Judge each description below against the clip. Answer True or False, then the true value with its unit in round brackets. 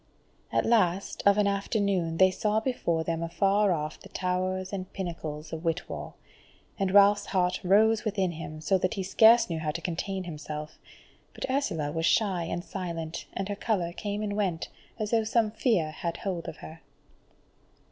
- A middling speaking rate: True (175 wpm)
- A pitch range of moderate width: True (3.6 semitones)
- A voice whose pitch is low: False (185 Hz)